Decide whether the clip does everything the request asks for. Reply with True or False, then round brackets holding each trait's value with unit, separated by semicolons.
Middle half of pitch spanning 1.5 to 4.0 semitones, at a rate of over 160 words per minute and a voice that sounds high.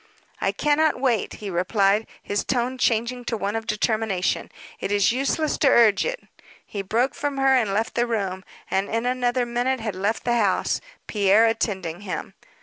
True (3.7 semitones; 175 wpm; 225 Hz)